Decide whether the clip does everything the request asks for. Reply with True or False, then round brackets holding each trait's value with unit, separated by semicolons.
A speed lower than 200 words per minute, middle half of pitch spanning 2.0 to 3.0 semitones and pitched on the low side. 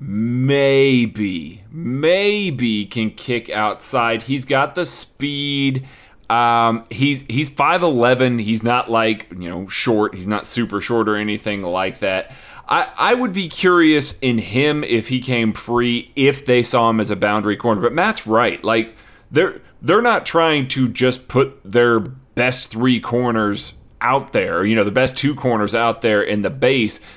False (165 wpm; 3.5 semitones; 120 Hz)